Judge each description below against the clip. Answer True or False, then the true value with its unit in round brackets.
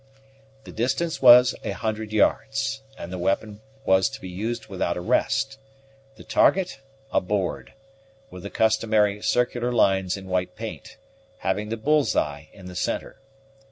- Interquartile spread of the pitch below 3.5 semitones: False (4.5 semitones)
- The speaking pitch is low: True (110 Hz)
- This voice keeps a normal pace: True (155 wpm)